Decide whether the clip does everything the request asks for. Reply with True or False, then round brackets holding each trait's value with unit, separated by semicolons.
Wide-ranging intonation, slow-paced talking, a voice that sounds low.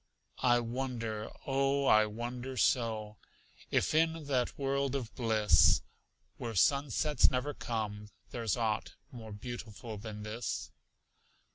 False (3.8 semitones; 115 wpm; 120 Hz)